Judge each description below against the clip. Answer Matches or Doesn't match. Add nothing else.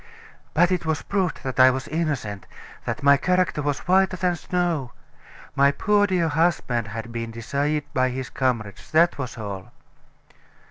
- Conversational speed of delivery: Matches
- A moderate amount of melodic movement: Doesn't match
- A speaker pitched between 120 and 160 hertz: Matches